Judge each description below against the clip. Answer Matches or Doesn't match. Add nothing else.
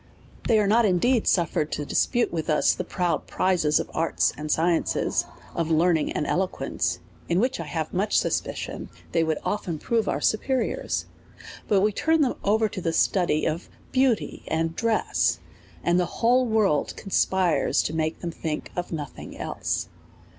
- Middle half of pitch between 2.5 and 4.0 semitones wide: Doesn't match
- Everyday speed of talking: Matches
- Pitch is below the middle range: Doesn't match